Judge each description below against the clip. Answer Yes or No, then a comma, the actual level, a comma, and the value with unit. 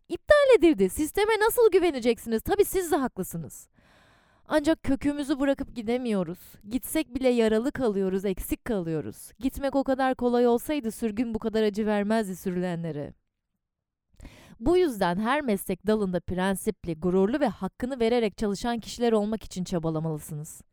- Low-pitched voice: No, high, 230 Hz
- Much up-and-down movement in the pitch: Yes, wide, 6.4 semitones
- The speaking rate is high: No, average, 130 wpm